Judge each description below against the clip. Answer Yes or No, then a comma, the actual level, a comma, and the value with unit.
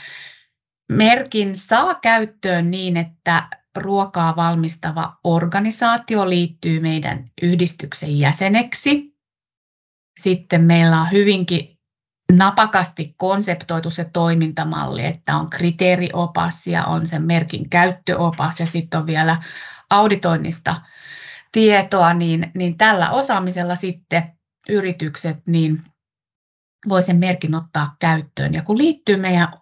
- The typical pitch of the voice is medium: Yes, medium, 175 Hz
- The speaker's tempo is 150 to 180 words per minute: No, average, 100 wpm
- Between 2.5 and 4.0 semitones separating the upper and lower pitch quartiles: Yes, average, 3.1 semitones